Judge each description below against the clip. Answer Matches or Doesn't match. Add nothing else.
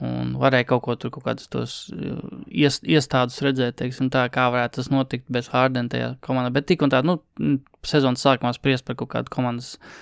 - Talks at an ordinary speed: Matches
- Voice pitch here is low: Matches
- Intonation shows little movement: Matches